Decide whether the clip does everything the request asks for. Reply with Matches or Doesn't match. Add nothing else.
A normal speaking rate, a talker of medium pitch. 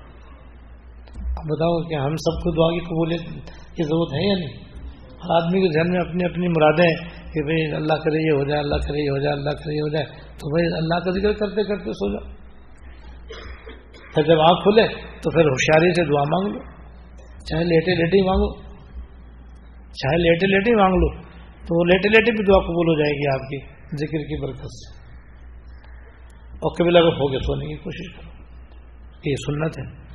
Doesn't match